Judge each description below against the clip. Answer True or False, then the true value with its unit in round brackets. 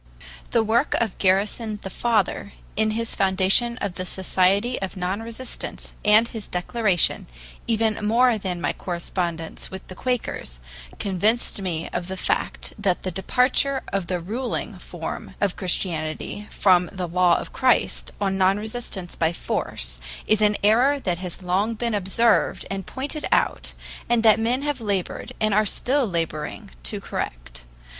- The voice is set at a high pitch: True (200 Hz)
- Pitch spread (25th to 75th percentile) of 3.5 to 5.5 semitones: True (4.0 semitones)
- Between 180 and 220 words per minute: False (155 wpm)